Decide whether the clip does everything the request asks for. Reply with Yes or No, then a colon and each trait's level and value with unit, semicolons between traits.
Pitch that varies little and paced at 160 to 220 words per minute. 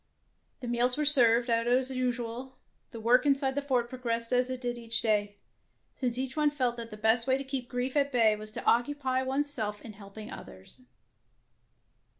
Yes: narrow, 2.3 semitones; average, 190 wpm